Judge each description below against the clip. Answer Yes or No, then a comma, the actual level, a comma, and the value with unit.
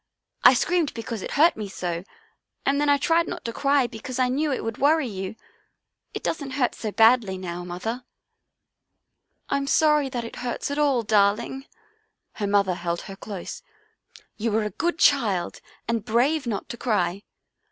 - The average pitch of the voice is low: No, high, 235 Hz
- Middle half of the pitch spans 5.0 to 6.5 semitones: Yes, wide, 5.6 semitones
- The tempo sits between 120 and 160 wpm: No, average, 175 wpm